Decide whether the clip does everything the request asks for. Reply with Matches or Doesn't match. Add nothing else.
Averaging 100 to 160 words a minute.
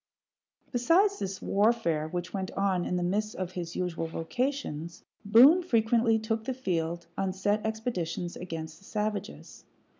Matches